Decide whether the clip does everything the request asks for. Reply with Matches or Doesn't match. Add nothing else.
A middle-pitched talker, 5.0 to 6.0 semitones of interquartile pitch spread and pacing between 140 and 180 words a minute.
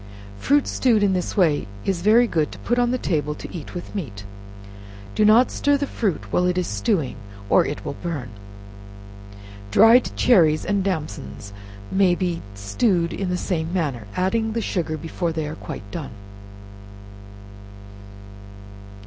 Matches